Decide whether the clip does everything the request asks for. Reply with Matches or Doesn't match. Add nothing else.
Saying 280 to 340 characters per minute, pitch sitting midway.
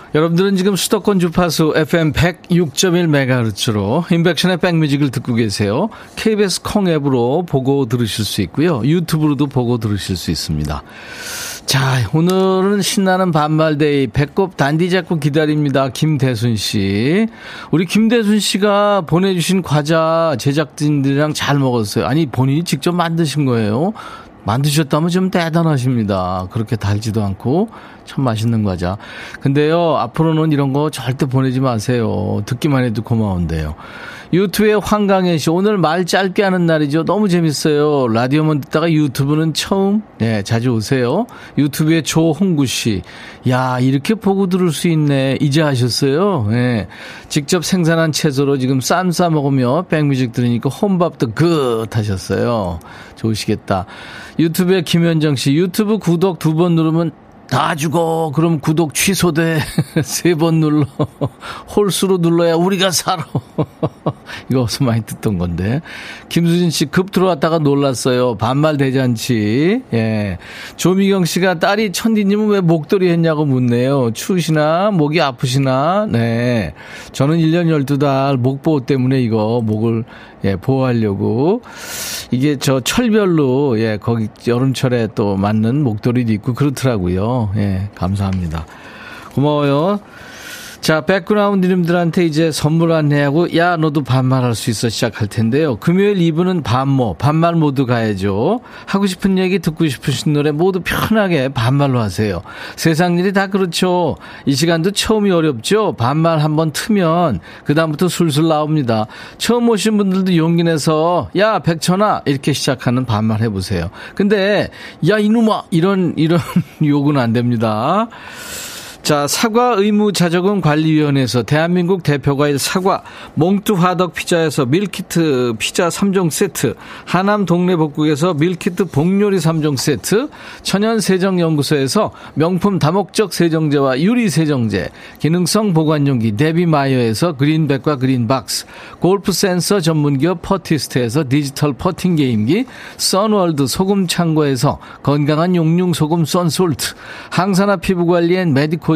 Matches